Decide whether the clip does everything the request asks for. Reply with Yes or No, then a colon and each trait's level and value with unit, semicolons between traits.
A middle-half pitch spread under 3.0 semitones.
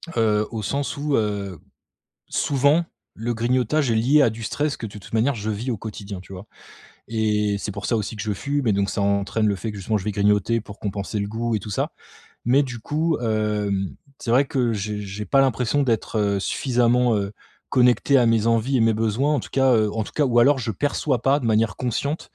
No: average, 3.7 semitones